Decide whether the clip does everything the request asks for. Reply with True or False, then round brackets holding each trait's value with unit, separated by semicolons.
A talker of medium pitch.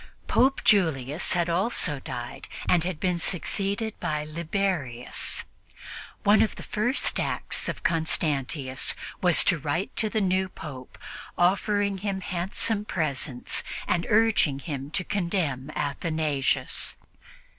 True (170 Hz)